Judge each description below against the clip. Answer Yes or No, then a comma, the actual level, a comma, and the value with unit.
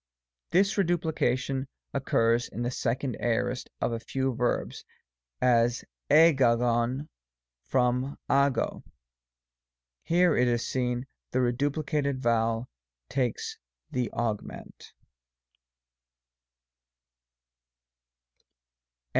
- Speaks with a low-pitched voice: Yes, low, 125 Hz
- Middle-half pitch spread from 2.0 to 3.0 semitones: Yes, narrow, 2.6 semitones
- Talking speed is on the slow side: Yes, slow, 80 wpm